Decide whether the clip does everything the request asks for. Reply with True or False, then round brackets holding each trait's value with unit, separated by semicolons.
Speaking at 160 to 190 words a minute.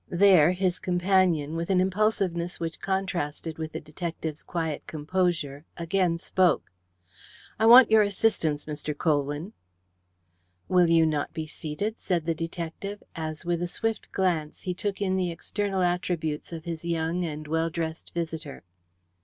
False (145 wpm)